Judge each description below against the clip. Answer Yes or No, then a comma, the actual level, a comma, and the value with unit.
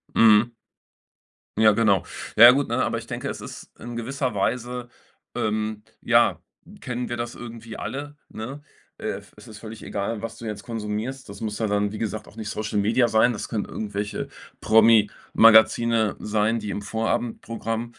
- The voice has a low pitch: Yes, low, 110 Hz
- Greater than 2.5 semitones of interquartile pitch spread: No, narrow, 1.8 semitones